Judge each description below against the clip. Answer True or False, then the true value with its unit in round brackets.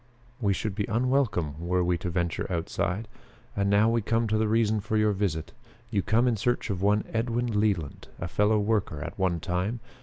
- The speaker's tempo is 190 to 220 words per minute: True (200 wpm)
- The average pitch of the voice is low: True (105 Hz)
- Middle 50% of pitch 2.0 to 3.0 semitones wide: False (3.7 semitones)